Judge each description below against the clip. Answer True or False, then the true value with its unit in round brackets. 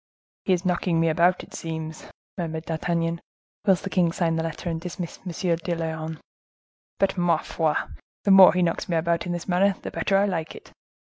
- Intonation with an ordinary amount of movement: False (1.9 semitones)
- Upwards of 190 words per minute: True (200 wpm)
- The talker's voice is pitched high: False (170 Hz)